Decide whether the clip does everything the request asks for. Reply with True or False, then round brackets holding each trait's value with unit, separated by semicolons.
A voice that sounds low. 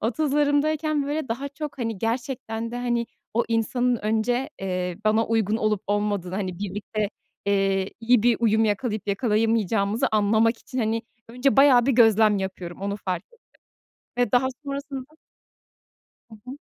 False (225 Hz)